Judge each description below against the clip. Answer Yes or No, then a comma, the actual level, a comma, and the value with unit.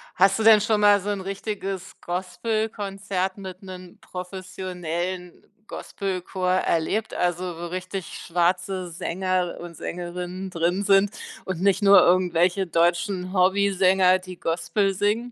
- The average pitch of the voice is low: No, medium, 185 Hz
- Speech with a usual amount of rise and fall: No, narrow, 1.8 semitones